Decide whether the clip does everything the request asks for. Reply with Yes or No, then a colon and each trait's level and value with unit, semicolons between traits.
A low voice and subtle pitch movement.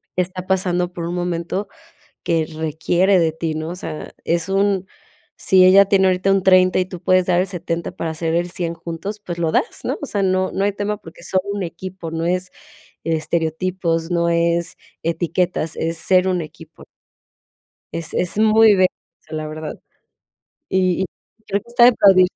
No: medium, 180 Hz; narrow, 2.2 semitones